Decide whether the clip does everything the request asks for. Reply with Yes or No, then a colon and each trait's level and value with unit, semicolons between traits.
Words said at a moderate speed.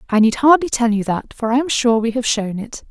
No: fast, 290 wpm